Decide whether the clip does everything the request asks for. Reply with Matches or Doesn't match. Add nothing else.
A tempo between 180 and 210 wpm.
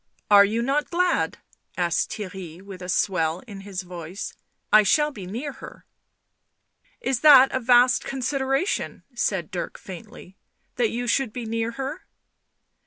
Doesn't match